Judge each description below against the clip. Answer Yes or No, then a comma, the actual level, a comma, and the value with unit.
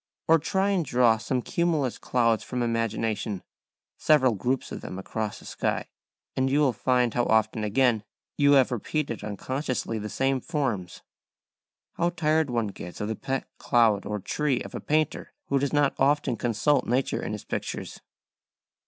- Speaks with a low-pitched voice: Yes, low, 125 Hz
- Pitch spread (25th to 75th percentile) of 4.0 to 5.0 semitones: Yes, average, 4.4 semitones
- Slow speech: No, average, 165 wpm